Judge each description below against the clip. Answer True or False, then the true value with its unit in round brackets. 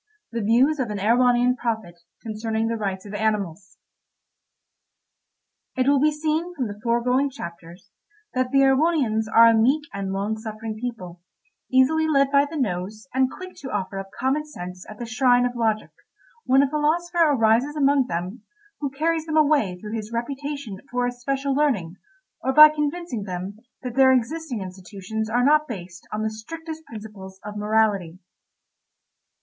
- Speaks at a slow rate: False (160 wpm)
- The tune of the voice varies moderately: True (5.0 semitones)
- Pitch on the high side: True (240 Hz)